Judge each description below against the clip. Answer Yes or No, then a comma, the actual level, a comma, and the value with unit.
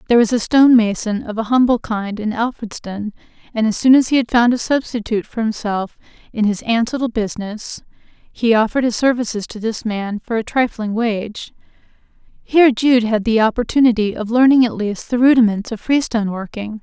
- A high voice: Yes, high, 225 Hz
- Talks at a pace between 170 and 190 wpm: Yes, average, 185 wpm